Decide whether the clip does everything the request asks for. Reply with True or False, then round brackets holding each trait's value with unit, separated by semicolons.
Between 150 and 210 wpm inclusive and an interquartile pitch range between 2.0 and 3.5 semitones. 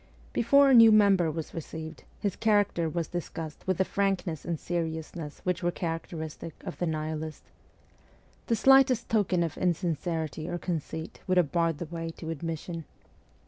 True (160 wpm; 2.9 semitones)